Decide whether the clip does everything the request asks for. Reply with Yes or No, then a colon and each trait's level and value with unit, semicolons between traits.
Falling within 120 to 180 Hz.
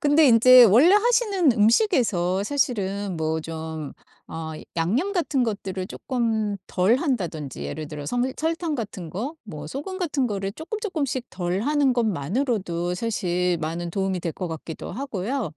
No: high, 210 Hz